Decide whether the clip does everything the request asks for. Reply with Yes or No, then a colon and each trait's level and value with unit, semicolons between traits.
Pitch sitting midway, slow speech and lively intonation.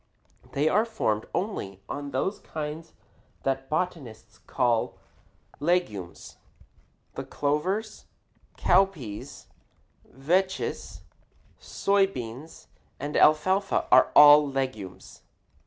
Yes: medium, 150 Hz; slow, 85 wpm; wide, 6.1 semitones